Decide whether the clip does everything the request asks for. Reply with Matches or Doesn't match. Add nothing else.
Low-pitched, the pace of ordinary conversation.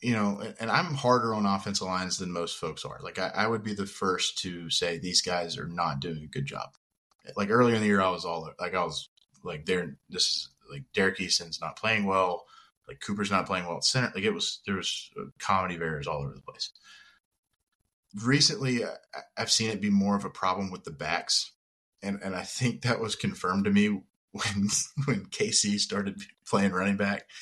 Doesn't match